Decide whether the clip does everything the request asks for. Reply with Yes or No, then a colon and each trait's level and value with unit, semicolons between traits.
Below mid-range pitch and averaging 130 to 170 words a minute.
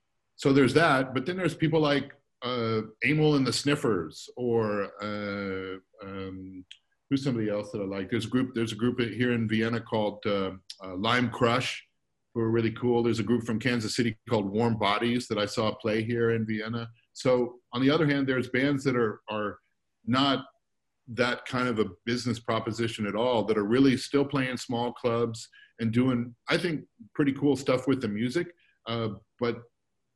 No: low, 120 Hz; average, 185 wpm